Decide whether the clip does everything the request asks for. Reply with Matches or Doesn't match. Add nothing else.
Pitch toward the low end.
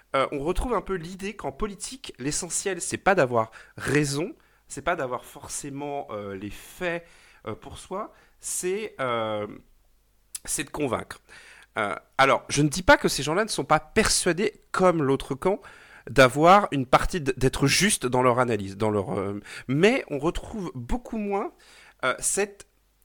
Doesn't match